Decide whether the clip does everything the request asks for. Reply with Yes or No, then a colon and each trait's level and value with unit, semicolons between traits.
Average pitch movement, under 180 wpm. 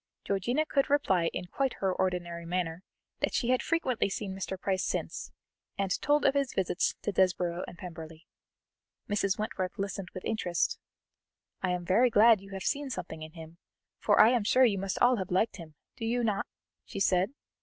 No: average, 4.4 semitones; average, 185 wpm